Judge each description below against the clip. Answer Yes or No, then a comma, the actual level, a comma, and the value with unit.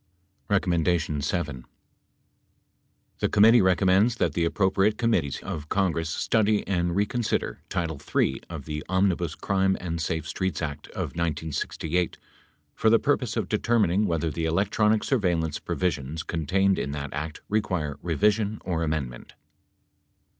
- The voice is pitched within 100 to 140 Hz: No, very low, 85 Hz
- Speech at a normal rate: No, slow, 125 wpm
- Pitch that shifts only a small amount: No, average, 4.2 semitones